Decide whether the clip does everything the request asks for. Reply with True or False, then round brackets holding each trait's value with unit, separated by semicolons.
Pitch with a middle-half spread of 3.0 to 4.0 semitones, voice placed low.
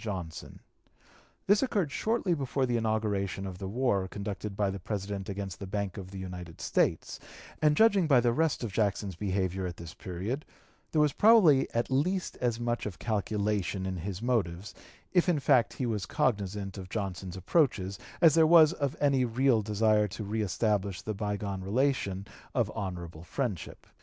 False (5.4 semitones; 105 Hz)